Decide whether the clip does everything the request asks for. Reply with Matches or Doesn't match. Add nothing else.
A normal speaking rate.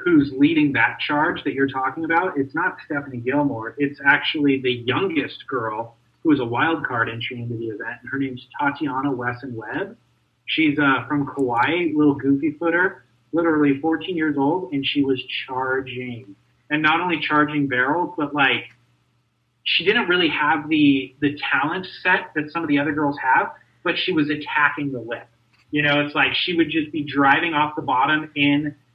Matches